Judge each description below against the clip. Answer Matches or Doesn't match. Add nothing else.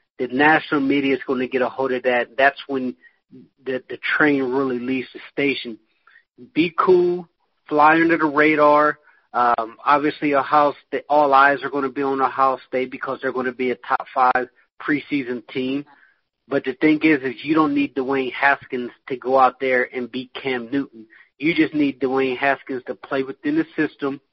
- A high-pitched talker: Doesn't match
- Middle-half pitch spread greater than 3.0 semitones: Doesn't match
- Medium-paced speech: Matches